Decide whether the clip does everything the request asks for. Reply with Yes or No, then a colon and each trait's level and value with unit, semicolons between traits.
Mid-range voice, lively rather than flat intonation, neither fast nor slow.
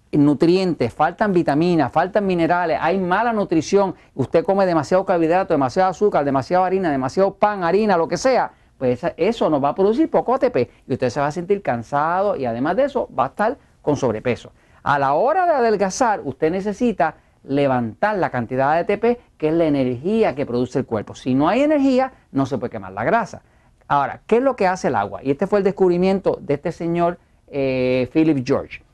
No: medium, 170 Hz; wide, 6.4 semitones; fast, 195 wpm